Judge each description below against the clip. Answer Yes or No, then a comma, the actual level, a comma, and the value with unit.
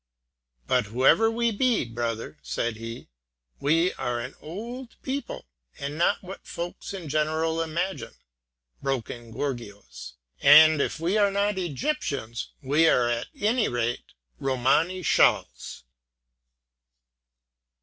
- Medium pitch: Yes, medium, 155 Hz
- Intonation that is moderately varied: No, wide, 8.0 semitones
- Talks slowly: Yes, slow, 115 wpm